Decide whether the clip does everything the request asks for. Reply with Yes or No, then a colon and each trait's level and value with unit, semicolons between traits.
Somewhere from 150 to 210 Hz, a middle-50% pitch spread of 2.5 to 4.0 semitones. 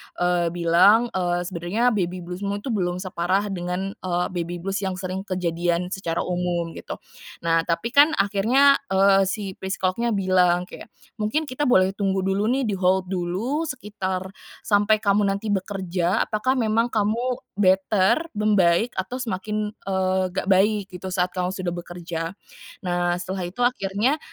Yes: high, 190 Hz; average, 2.9 semitones